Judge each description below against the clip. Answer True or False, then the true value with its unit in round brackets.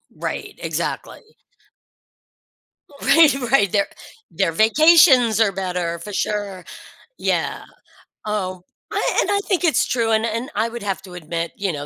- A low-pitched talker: False (210 Hz)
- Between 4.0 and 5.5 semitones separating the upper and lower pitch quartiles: True (4.5 semitones)